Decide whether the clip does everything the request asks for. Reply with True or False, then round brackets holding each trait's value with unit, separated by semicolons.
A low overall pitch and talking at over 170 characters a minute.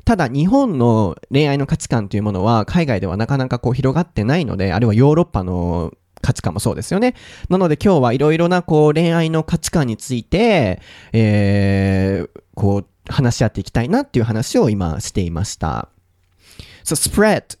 True (115 Hz; 385 characters per minute)